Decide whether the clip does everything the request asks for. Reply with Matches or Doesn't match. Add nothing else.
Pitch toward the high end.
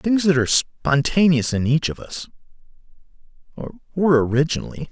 Doesn't match